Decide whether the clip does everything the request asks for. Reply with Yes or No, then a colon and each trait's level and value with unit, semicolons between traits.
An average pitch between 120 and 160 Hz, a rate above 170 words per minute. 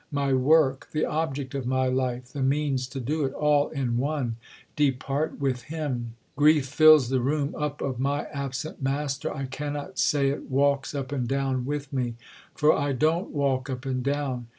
Yes: medium, 140 Hz; average, 180 wpm